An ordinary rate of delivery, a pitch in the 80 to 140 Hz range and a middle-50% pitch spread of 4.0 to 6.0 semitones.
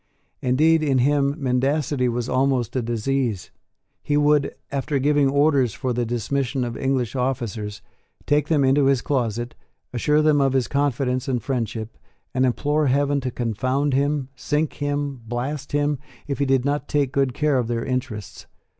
No: average, 165 wpm; low, 135 Hz; average, 2.7 semitones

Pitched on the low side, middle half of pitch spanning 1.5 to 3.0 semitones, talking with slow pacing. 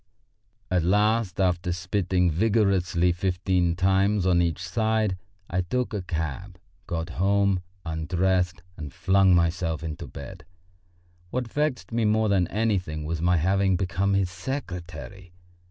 Yes: very low, 90 Hz; narrow, 2.5 semitones; slow, 130 wpm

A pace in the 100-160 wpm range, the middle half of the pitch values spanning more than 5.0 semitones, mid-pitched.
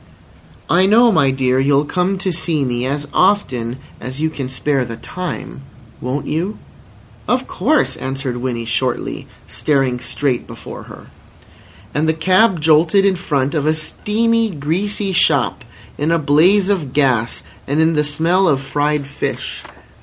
Yes: average, 155 wpm; wide, 5.5 semitones; medium, 150 Hz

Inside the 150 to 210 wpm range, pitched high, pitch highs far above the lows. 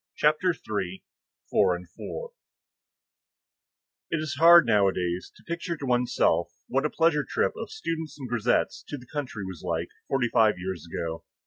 No: average, 155 wpm; low, 120 Hz; wide, 8.7 semitones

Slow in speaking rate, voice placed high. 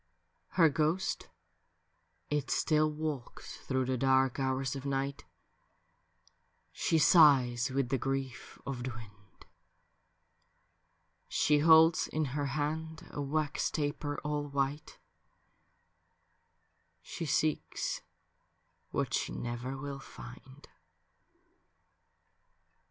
No: slow, 95 wpm; medium, 140 Hz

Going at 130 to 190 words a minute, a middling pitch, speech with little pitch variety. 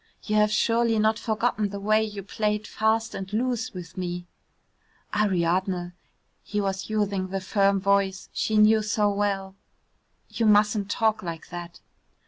No: average, 145 wpm; high, 205 Hz; narrow, 2.1 semitones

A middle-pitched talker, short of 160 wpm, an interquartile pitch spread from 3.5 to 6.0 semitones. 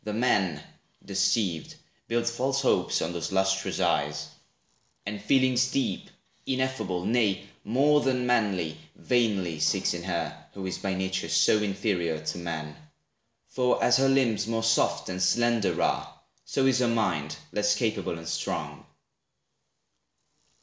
No: low, 105 Hz; slow, 135 wpm; average, 5.0 semitones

